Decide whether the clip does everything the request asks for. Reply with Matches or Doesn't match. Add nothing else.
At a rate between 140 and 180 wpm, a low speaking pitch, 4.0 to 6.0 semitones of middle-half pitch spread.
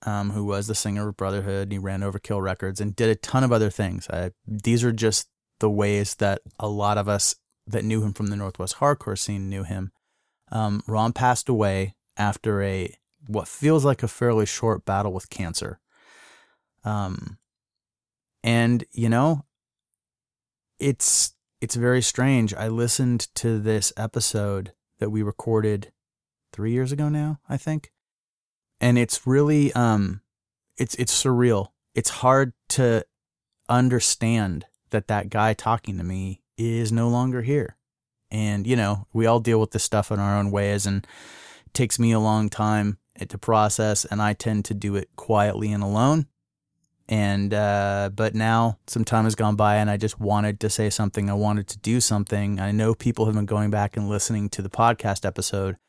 Doesn't match